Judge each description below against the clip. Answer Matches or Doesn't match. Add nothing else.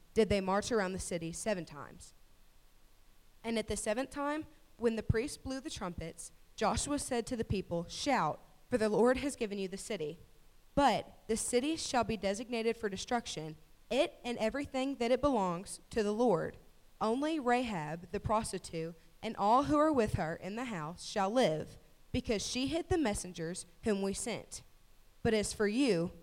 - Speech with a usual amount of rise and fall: Matches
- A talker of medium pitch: Doesn't match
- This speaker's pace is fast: Doesn't match